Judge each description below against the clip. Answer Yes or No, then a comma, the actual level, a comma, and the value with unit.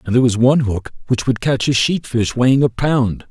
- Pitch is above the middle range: No, low, 125 Hz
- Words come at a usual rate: No, fast, 255 wpm